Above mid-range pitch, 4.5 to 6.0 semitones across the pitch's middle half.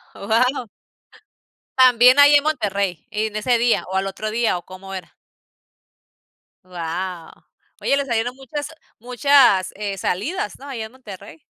Yes: high, 220 Hz; average, 5.2 semitones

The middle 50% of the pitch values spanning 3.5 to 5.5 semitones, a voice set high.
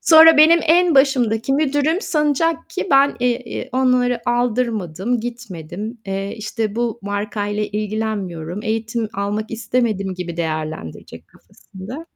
Yes: average, 4.6 semitones; high, 225 Hz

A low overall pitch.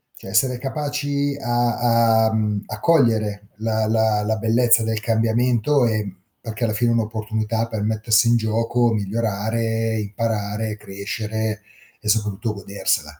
Yes: low, 110 Hz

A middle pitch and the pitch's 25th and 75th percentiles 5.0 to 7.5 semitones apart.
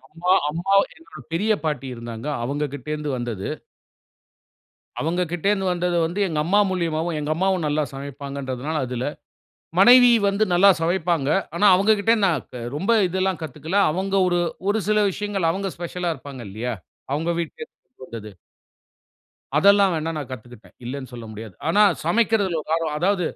Yes: medium, 165 Hz; wide, 5.5 semitones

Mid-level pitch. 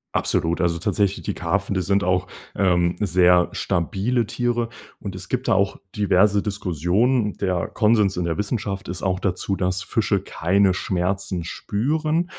No: very low, 95 Hz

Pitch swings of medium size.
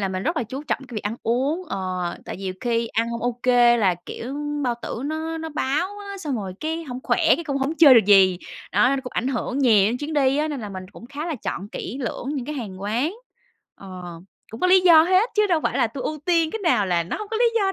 No: wide, 6.5 semitones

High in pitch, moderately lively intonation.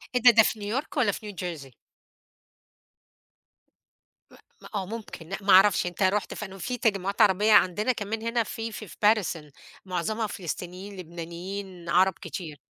Yes: high, 195 Hz; average, 3.4 semitones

